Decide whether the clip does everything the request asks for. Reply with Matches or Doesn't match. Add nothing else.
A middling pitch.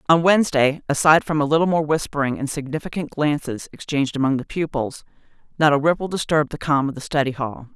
Matches